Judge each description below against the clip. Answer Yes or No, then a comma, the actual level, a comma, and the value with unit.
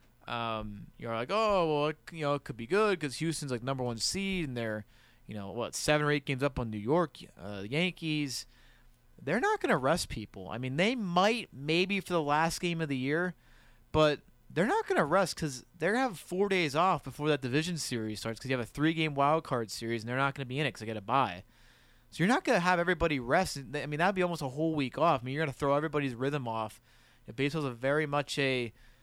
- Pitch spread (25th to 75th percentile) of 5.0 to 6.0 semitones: Yes, average, 5.3 semitones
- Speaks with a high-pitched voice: No, medium, 145 Hz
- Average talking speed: No, fast, 265 wpm